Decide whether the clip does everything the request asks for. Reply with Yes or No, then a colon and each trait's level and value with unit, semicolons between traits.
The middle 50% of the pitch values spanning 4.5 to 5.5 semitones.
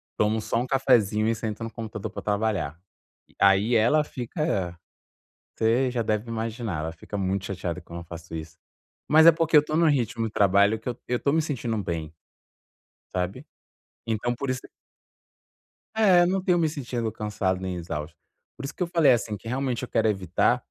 Yes: average, 5.1 semitones